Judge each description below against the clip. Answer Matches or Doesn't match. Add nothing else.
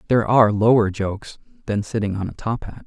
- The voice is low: Matches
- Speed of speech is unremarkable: Doesn't match